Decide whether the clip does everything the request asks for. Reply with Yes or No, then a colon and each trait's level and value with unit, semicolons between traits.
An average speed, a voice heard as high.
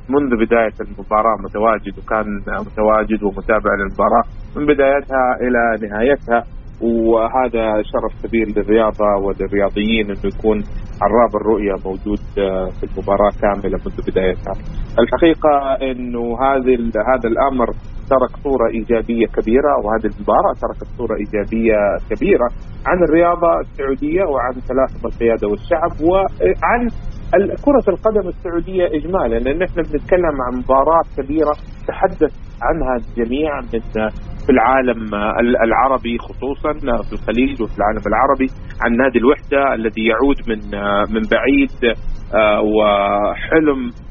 No: average, 110 wpm; low, 115 Hz